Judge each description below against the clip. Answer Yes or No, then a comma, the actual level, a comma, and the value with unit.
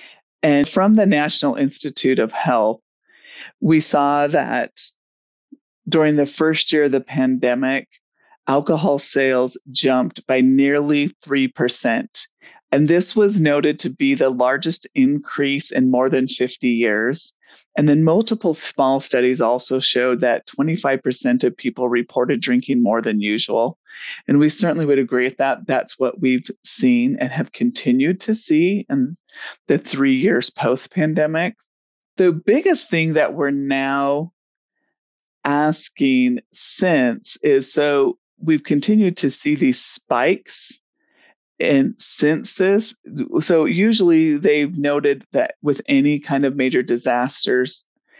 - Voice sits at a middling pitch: Yes, medium, 150 Hz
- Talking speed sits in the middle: No, slow, 130 wpm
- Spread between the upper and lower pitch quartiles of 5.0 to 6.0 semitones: No, wide, 8.5 semitones